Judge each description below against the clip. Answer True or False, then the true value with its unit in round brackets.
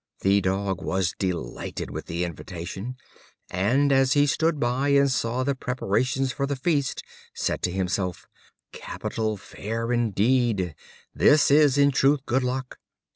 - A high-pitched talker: False (125 Hz)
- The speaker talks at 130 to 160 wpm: True (140 wpm)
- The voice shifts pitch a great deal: True (6.1 semitones)